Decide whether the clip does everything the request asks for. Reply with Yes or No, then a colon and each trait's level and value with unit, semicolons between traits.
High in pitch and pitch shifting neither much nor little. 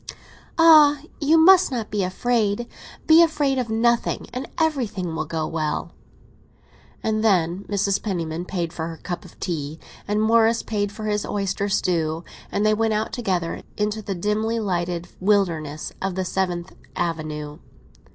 Yes: high, 200 Hz; average, 4.7 semitones